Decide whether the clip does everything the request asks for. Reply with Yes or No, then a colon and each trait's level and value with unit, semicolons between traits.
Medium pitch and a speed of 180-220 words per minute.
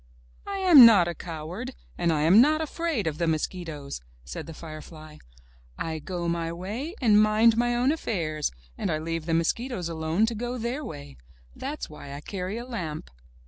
Yes: medium, 180 Hz; average, 185 wpm